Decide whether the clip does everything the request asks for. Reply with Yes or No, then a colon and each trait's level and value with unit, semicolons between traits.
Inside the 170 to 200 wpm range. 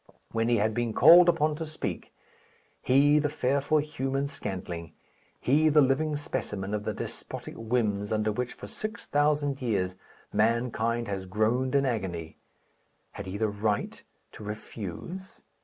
No: average, 145 wpm